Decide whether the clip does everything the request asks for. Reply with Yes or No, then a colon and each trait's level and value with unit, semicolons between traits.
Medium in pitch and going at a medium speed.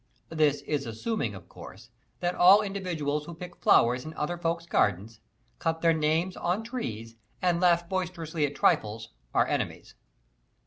Yes: medium, 165 Hz; average, 150 wpm